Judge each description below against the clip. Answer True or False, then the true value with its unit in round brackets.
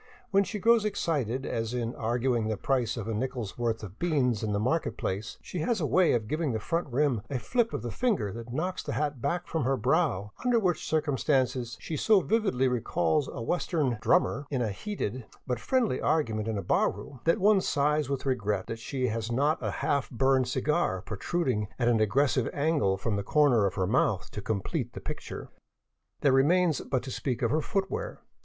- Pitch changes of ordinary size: False (5.8 semitones)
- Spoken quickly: True (210 wpm)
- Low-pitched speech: True (130 Hz)